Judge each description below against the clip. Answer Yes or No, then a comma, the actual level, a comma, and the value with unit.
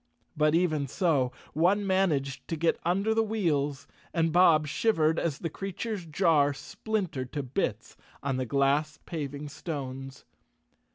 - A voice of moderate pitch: Yes, medium, 155 Hz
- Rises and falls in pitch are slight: No, average, 4.4 semitones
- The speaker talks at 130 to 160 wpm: Yes, average, 145 wpm